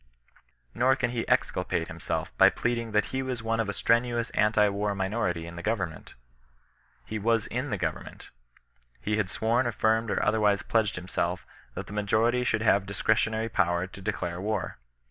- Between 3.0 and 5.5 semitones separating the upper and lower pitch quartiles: No, narrow, 2.6 semitones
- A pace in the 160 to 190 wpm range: Yes, average, 180 wpm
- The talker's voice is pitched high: No, low, 110 Hz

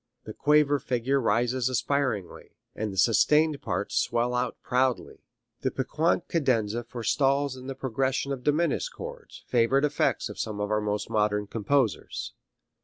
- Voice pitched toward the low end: Yes, low, 130 Hz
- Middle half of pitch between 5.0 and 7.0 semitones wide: No, average, 4.0 semitones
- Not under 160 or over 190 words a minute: No, average, 145 wpm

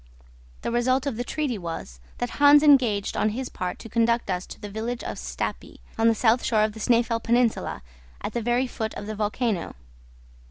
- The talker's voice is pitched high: Yes, high, 230 Hz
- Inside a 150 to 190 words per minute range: No, average, 200 wpm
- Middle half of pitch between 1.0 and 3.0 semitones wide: Yes, narrow, 2.4 semitones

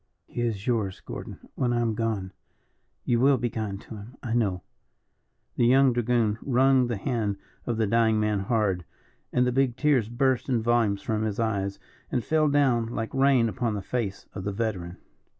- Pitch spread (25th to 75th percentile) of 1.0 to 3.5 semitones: Yes, average, 2.9 semitones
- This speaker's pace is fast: No, average, 185 wpm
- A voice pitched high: No, low, 115 Hz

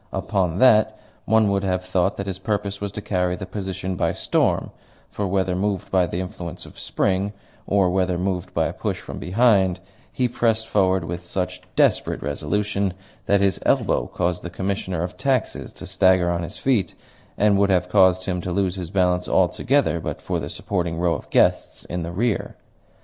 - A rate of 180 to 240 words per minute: Yes, average, 190 wpm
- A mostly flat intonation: Yes, narrow, 2.0 semitones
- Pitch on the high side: No, very low, 95 Hz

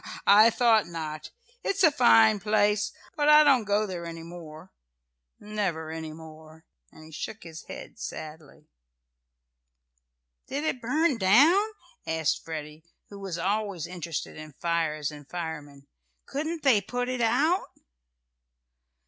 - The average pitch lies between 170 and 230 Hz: Yes, high, 190 Hz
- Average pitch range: No, wide, 6.5 semitones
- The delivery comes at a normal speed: No, slow, 130 wpm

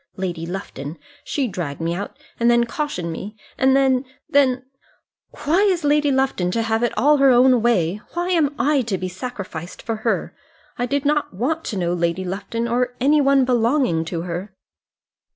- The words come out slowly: No, average, 180 wpm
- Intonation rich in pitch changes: Yes, wide, 7.0 semitones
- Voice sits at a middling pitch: No, high, 235 Hz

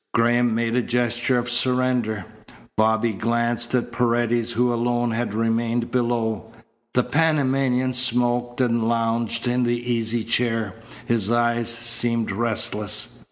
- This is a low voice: Yes, low, 120 Hz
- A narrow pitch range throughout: Yes, narrow, 1.1 semitones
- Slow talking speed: Yes, slow, 125 wpm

